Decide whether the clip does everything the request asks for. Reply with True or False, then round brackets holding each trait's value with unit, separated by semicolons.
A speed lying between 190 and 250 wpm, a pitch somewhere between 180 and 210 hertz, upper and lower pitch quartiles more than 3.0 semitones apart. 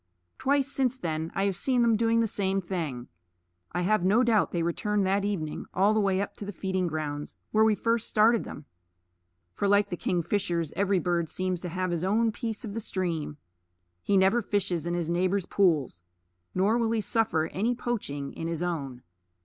True (195 wpm; 190 Hz; 4.0 semitones)